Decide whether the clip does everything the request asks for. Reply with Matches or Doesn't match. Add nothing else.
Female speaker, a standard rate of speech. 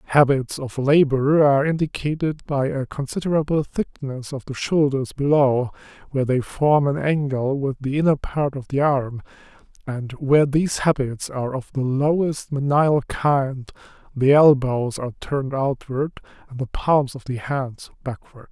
Doesn't match